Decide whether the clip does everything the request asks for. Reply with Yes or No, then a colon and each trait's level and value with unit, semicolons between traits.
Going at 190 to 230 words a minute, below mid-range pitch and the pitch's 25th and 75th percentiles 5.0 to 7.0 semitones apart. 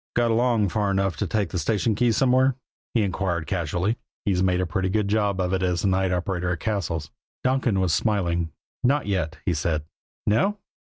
No: average, 195 wpm; very low, 95 Hz; average, 3.6 semitones